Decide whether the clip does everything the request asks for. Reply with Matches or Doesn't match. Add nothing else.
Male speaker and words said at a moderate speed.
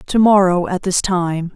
Doesn't match